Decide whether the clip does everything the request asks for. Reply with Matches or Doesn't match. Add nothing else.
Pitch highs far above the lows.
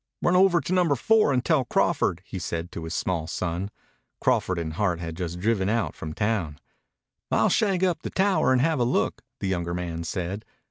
Matches